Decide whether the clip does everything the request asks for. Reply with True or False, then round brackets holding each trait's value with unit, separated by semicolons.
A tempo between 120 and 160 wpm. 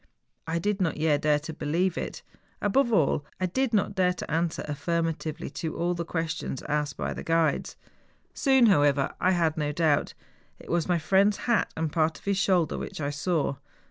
False (195 wpm)